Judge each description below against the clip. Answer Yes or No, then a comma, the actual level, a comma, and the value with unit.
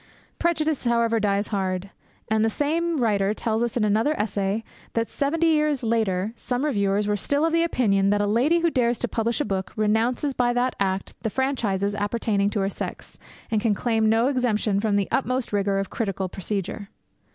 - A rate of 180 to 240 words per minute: Yes, average, 185 wpm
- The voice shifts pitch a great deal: No, average, 3.9 semitones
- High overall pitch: Yes, high, 220 Hz